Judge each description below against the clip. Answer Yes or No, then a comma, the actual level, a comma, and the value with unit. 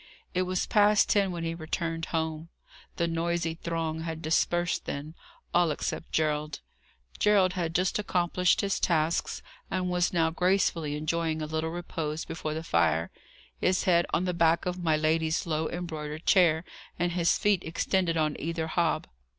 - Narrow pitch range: Yes, narrow, 2.0 semitones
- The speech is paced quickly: No, average, 160 wpm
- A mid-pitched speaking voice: Yes, medium, 165 Hz